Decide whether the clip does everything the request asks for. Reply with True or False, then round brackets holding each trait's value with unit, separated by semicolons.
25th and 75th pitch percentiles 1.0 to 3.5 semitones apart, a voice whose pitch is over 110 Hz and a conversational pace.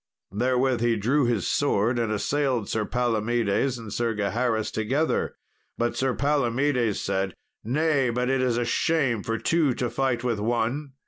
True (2.9 semitones; 120 Hz; 155 wpm)